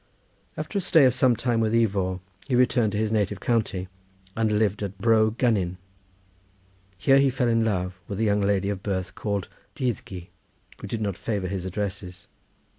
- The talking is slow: No, average, 180 wpm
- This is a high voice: No, low, 105 Hz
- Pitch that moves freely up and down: No, average, 3.3 semitones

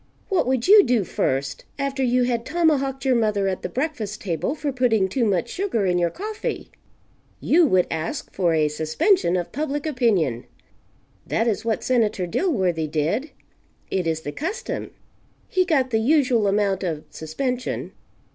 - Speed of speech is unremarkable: Yes, average, 160 wpm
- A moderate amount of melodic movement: No, wide, 7.6 semitones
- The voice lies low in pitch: No, high, 230 Hz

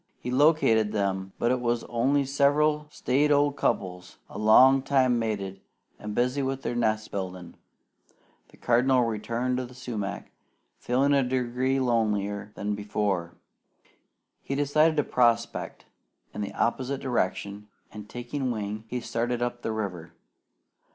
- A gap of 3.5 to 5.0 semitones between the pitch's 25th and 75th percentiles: Yes, average, 4.0 semitones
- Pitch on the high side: No, low, 120 Hz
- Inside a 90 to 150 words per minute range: Yes, average, 140 wpm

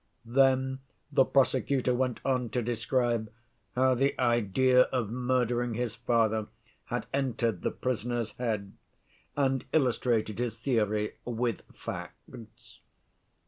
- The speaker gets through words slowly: Yes, slow, 110 wpm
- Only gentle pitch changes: Yes, narrow, 2.2 semitones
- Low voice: Yes, low, 120 Hz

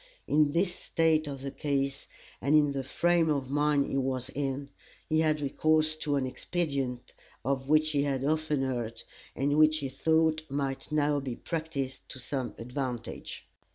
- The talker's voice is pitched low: No, medium, 145 Hz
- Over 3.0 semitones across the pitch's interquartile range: No, narrow, 2.5 semitones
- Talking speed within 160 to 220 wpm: Yes, average, 165 wpm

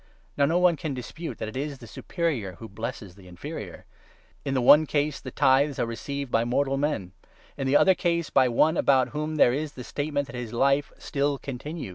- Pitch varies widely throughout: No, average, 3.7 semitones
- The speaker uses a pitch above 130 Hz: Yes, medium, 140 Hz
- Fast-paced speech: Yes, fast, 220 wpm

